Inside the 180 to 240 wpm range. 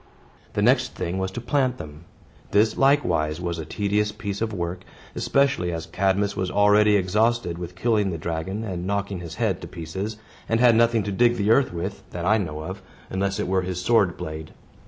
Yes: average, 200 wpm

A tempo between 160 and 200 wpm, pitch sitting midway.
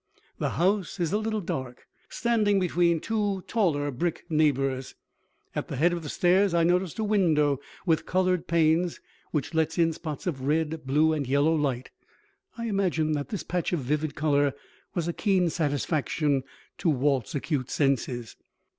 Yes: average, 165 wpm; medium, 160 Hz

